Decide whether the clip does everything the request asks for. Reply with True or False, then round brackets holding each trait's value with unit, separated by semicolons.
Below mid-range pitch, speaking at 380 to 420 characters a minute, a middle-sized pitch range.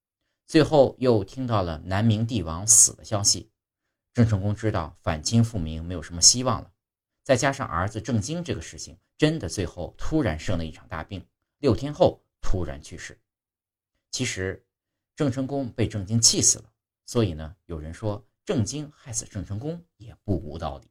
False (110 Hz; 255 characters per minute; 4.7 semitones)